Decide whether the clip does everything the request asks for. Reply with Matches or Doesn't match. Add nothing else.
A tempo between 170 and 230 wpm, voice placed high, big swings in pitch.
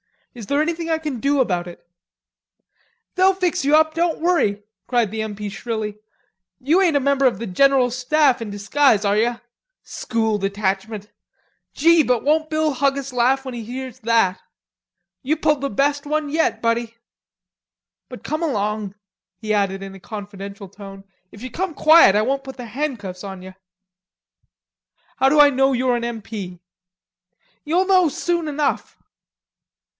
Doesn't match